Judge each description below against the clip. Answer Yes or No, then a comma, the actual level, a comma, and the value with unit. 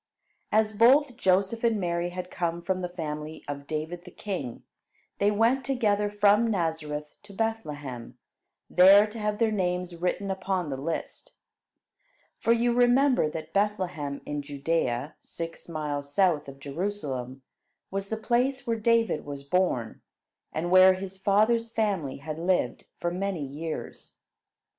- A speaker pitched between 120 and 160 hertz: No, medium, 180 Hz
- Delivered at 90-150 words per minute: Yes, average, 145 wpm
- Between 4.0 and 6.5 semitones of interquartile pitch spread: Yes, wide, 5.6 semitones